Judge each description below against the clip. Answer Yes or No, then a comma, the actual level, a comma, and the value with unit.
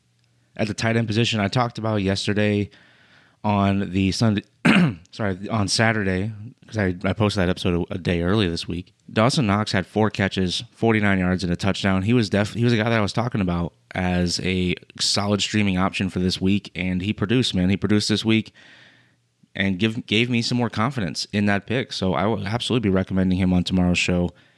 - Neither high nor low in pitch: No, low, 100 Hz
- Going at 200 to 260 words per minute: Yes, fast, 205 wpm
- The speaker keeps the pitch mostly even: No, average, 3.2 semitones